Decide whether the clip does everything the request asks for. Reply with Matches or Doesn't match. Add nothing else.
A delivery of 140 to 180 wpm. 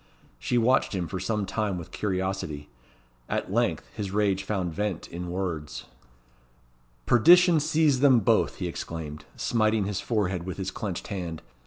Matches